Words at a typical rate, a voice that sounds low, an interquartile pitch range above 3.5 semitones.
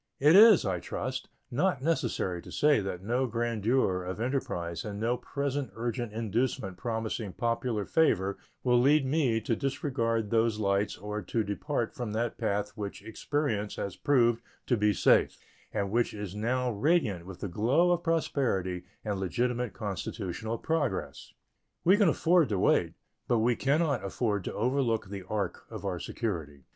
Yes: average, 160 wpm; low, 115 Hz; average, 4.5 semitones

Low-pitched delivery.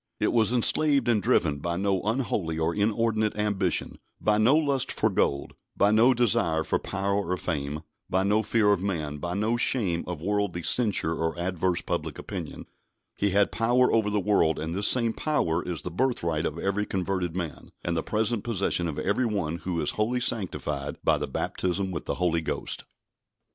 Yes: low, 100 Hz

